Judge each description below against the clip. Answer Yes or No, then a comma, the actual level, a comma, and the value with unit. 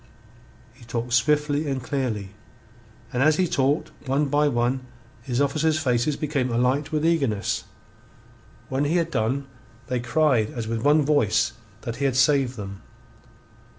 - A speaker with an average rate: Yes, average, 150 wpm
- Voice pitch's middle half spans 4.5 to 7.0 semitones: No, average, 3.8 semitones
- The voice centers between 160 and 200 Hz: No, low, 135 Hz